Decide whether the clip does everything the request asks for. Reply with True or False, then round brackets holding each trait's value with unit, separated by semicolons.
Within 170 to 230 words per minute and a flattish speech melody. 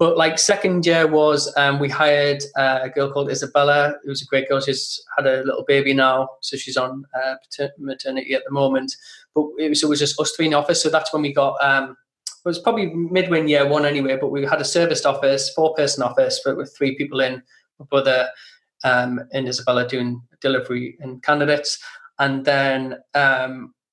True (200 wpm; 2.2 semitones)